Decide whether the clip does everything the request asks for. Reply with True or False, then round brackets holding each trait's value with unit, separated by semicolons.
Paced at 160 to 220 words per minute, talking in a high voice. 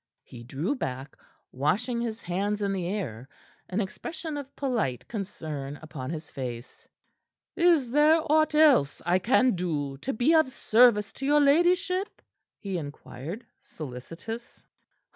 False (135 wpm; 205 Hz)